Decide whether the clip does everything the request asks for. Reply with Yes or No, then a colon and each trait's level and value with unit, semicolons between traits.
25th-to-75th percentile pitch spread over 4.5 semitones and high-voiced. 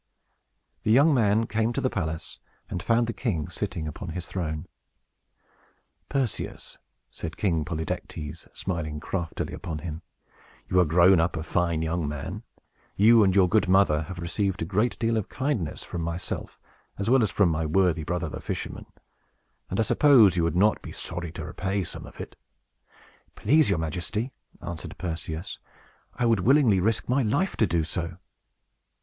No: average, 5.0 semitones; very low, 90 Hz